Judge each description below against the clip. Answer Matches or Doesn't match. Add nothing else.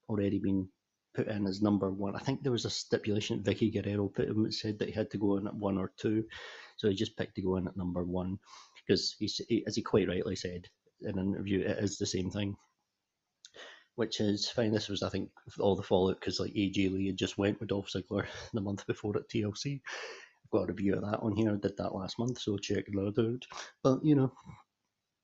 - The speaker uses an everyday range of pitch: Doesn't match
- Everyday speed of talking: Doesn't match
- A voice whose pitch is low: Matches